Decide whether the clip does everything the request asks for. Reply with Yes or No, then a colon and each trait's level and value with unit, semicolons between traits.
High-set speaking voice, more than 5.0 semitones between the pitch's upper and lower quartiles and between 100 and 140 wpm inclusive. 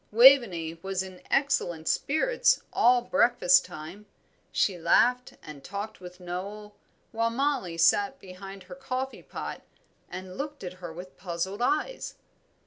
Yes: high, 195 Hz; wide, 5.4 semitones; slow, 135 wpm